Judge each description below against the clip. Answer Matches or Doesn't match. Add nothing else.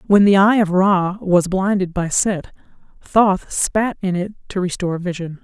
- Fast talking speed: Doesn't match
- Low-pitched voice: Doesn't match